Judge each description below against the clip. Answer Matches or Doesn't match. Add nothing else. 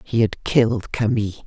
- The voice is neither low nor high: Doesn't match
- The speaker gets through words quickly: Doesn't match